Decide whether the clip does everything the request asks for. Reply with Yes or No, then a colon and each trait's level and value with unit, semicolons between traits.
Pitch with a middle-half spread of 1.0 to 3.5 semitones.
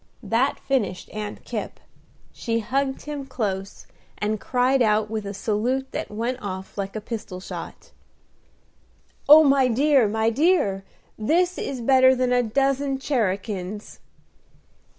No: average, 4.4 semitones